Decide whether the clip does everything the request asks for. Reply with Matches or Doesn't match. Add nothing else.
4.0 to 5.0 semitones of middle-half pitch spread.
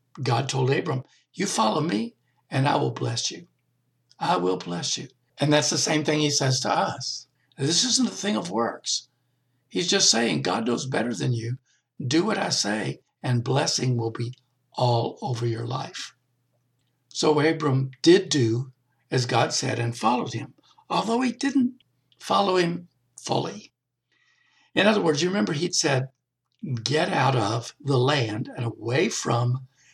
Doesn't match